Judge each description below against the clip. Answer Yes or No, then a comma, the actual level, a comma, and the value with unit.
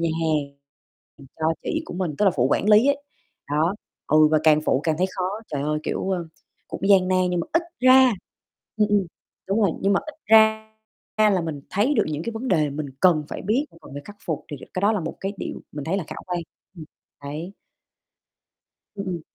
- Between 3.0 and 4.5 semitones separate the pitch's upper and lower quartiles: No, average, 5.2 semitones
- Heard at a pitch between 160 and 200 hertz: Yes, medium, 185 Hz